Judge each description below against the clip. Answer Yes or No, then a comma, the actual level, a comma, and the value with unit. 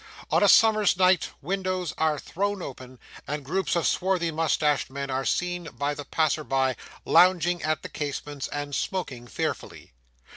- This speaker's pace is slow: No, average, 155 wpm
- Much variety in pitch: No, average, 4.4 semitones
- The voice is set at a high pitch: No, medium, 160 Hz